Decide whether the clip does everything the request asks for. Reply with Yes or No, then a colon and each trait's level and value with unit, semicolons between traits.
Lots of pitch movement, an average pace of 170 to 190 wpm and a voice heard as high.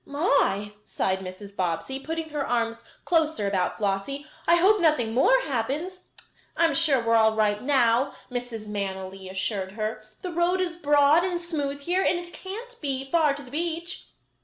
Yes: wide, 7.7 semitones; average, 175 wpm; very high, 275 Hz